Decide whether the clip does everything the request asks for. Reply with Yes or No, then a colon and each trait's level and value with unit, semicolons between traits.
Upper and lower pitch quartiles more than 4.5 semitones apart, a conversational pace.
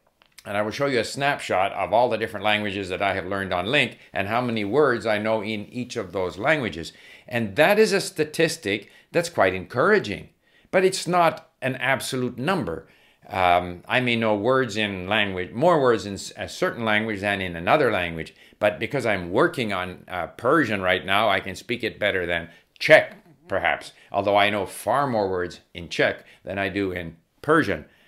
Yes: average, 5.0 semitones; average, 190 wpm